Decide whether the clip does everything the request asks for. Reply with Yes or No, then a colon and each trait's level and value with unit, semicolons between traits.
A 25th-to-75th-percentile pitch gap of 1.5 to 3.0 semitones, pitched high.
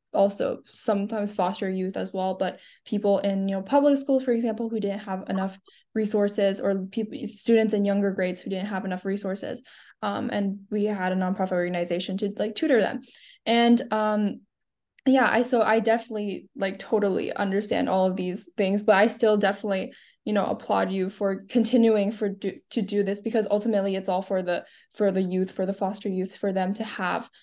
Yes: narrow, 2.4 semitones; high, 200 Hz